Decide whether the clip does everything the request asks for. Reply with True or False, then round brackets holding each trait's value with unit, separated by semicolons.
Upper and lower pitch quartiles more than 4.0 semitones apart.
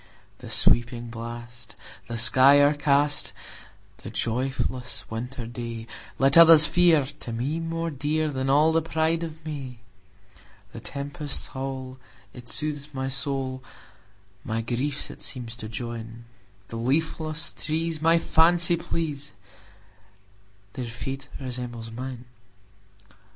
True (4.5 semitones)